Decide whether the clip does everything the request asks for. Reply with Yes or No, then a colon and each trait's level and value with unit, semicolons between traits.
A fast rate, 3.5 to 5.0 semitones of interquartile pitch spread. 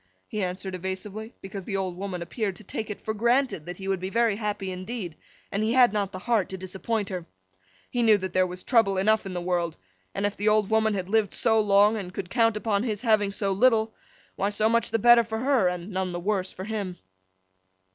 No: fast, 230 wpm; average, 2.8 semitones